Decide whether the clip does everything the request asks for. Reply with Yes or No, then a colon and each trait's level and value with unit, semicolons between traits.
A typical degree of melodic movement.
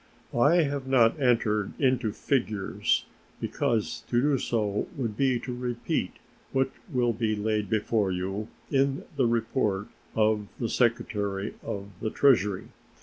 Yes: average, 3.8 semitones